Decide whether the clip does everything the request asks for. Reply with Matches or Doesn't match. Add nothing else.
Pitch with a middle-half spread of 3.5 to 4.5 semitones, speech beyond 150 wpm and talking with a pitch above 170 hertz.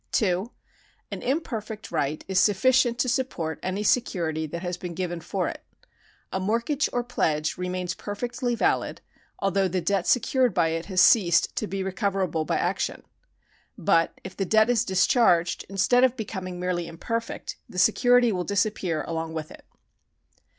Doesn't match